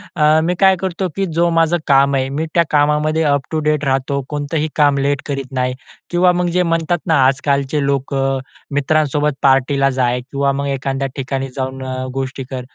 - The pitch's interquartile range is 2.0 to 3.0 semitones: Yes, narrow, 2.5 semitones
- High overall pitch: No, medium, 140 Hz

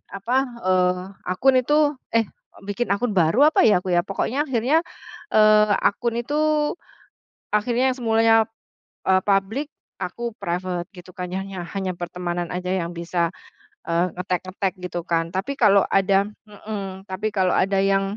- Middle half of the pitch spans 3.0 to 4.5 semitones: Yes, average, 4.0 semitones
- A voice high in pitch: Yes, high, 195 Hz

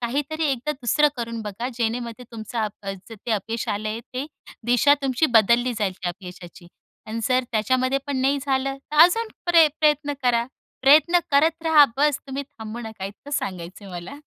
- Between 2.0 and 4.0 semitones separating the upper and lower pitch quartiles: No, average, 4.5 semitones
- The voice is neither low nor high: No, very high, 250 Hz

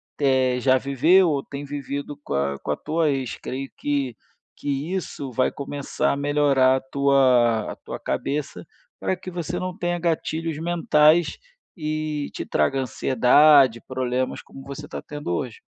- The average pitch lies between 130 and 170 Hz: Yes, medium, 140 Hz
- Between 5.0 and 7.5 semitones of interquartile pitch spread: No, average, 2.9 semitones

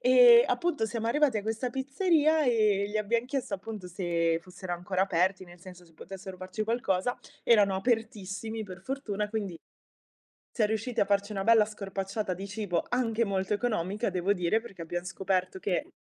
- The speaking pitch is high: Yes, high, 205 Hz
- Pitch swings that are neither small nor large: Yes, average, 3.6 semitones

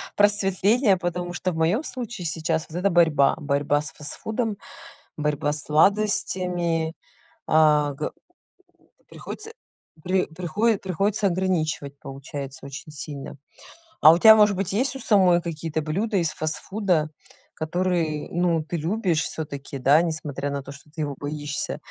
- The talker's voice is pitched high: No, medium, 165 Hz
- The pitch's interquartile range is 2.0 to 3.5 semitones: No, average, 4.1 semitones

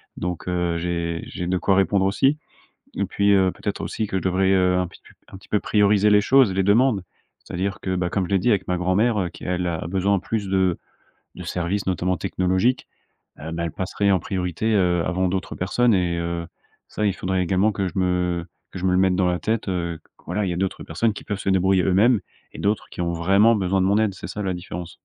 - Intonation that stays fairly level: Yes, narrow, 2.1 semitones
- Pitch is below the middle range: Yes, very low, 95 Hz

